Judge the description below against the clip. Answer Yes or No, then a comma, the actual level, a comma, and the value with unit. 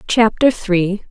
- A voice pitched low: No, high, 205 Hz